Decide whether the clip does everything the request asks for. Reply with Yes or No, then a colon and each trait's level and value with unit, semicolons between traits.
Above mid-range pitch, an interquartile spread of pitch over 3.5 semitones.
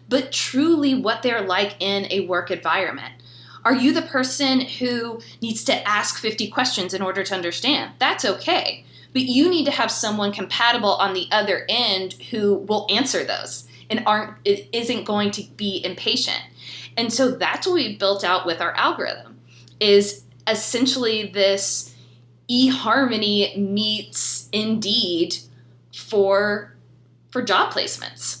Yes: high, 205 Hz; average, 4.3 semitones